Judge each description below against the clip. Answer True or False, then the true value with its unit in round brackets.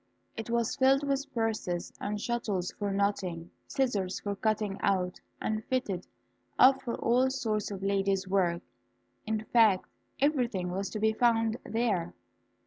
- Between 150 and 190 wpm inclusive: False (140 wpm)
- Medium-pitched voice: False (215 Hz)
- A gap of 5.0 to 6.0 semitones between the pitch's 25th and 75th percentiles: False (3.5 semitones)